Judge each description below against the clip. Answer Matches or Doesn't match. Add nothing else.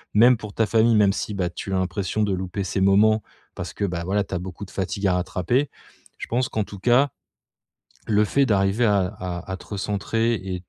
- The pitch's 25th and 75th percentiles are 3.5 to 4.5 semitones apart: Doesn't match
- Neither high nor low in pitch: Doesn't match